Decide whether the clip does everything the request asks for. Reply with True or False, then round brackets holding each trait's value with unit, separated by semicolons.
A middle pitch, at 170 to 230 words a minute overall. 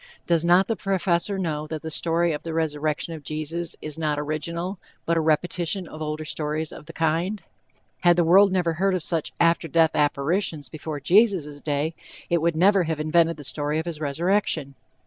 True (165 Hz; 190 wpm)